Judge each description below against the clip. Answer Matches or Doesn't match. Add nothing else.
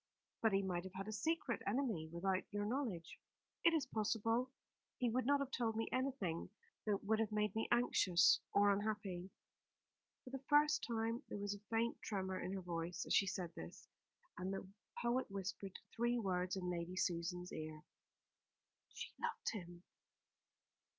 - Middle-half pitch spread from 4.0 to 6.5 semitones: Matches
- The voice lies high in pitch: Matches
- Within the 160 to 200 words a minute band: Matches